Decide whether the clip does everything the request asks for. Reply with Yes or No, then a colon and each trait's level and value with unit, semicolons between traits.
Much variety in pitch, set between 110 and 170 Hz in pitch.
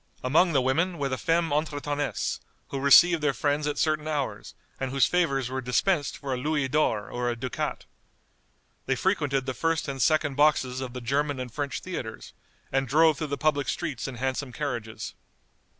No: average, 2.9 semitones; medium, 140 Hz